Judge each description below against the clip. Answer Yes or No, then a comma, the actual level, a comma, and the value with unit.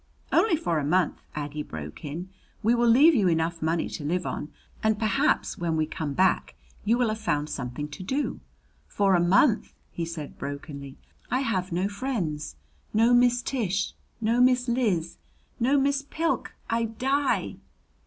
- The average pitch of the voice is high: Yes, high, 195 Hz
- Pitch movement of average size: No, wide, 7.4 semitones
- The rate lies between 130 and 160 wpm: No, average, 170 wpm